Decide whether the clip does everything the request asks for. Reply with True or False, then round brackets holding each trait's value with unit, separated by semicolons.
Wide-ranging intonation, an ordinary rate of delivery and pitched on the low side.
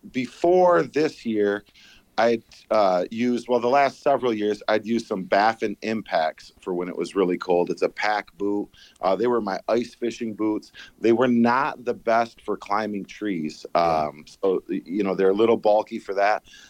False (2.9 semitones; 185 wpm; 110 Hz)